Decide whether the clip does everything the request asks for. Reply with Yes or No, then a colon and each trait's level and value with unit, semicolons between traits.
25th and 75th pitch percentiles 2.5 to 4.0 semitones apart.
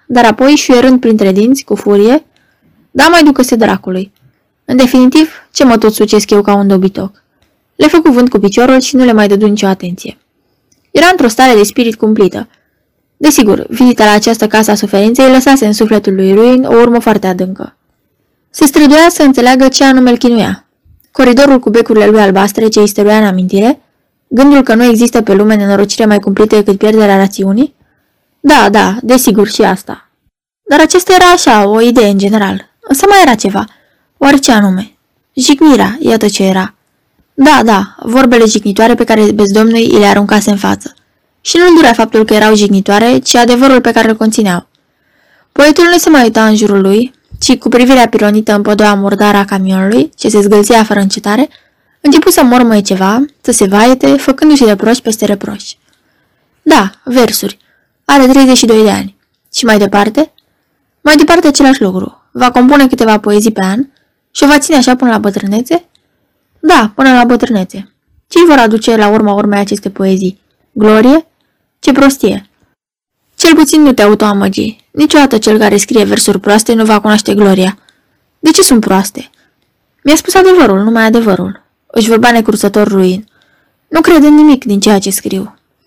No: average, 4.5 semitones